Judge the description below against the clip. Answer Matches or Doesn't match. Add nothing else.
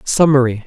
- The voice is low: Matches